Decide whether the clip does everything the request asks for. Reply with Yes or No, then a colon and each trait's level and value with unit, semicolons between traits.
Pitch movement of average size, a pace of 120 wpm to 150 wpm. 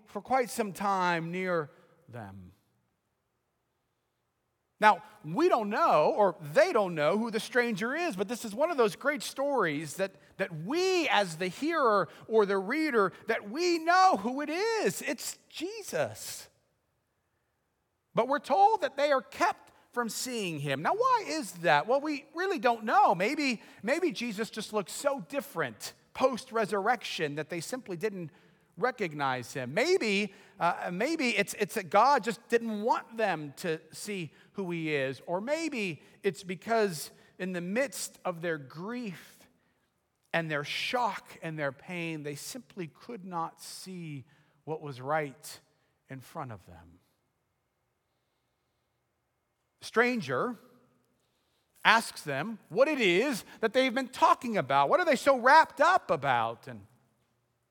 No: wide, 8.1 semitones; average, 145 wpm